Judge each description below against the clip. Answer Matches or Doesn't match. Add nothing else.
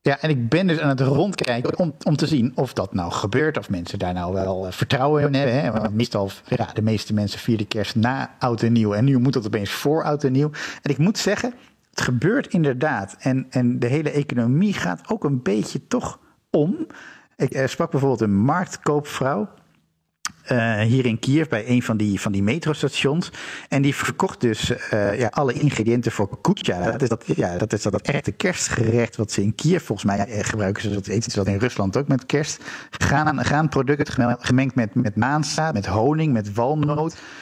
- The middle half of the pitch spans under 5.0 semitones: Doesn't match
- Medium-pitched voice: Doesn't match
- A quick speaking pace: Matches